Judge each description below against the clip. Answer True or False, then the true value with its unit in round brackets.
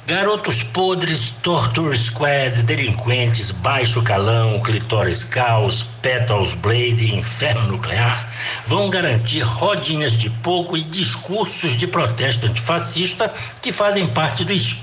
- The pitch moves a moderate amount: False (6.3 semitones)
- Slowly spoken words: True (110 wpm)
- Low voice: True (120 Hz)